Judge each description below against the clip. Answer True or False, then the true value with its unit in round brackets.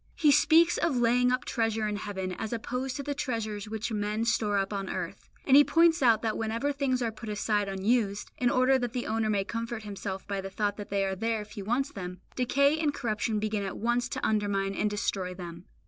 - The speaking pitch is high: True (220 Hz)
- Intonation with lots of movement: False (3.5 semitones)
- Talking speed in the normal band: False (225 wpm)